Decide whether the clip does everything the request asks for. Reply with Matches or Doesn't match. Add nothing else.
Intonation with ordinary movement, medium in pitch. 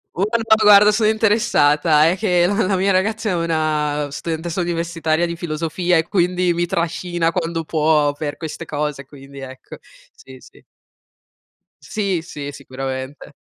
Matches